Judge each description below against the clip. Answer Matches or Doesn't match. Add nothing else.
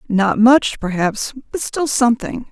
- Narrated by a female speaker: Matches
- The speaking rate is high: Doesn't match